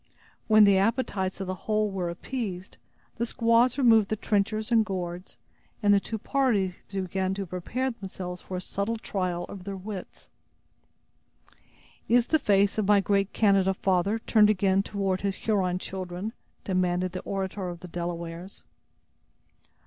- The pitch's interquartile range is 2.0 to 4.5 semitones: Yes, average, 2.7 semitones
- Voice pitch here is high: Yes, high, 195 Hz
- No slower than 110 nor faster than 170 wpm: Yes, average, 150 wpm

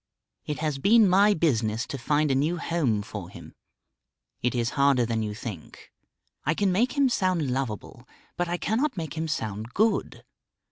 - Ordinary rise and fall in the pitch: No, wide, 7.7 semitones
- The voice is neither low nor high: Yes, medium, 150 Hz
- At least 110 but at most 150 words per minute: No, average, 175 wpm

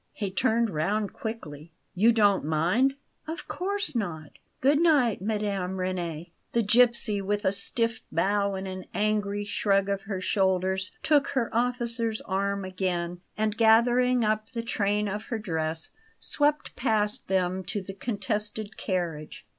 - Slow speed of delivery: No, average, 145 wpm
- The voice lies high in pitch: Yes, high, 205 Hz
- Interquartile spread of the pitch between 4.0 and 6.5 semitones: No, average, 3.5 semitones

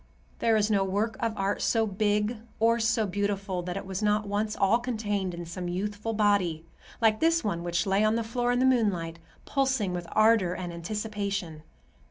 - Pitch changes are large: No, average, 3.1 semitones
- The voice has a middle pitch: No, high, 205 Hz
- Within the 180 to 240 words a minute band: Yes, average, 190 wpm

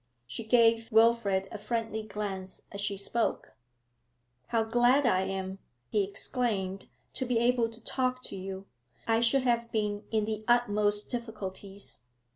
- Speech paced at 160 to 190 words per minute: No, average, 145 wpm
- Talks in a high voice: Yes, high, 220 Hz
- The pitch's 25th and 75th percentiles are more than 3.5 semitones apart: No, average, 2.9 semitones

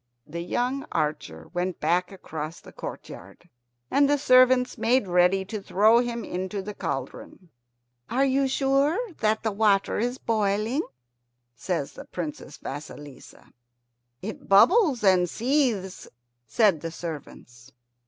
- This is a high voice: Yes, high, 200 Hz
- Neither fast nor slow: No, slow, 125 wpm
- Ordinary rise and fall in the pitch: No, wide, 6.5 semitones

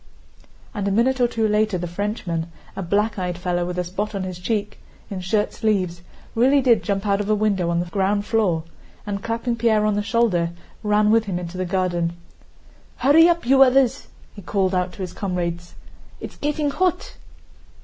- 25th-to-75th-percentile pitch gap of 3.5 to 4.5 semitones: Yes, average, 4.0 semitones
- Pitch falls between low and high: No, high, 205 Hz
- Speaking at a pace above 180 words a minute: Yes, average, 190 wpm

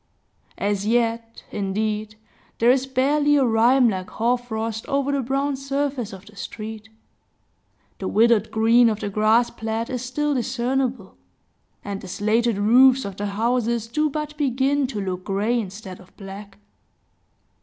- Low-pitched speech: No, high, 230 Hz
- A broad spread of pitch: No, average, 3.8 semitones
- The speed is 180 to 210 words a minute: No, average, 145 wpm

